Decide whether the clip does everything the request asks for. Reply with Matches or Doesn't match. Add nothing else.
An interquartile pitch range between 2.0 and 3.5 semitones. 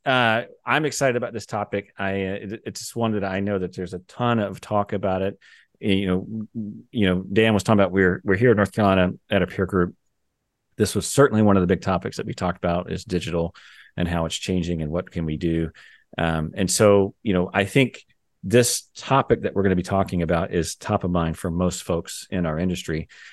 Matches